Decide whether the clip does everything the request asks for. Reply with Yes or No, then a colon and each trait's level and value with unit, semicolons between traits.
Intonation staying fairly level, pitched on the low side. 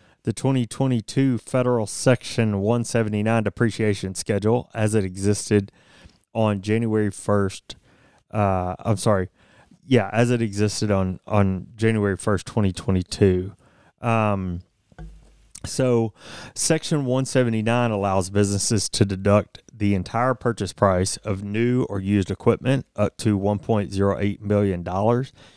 No: average, 3.0 semitones; low, 105 Hz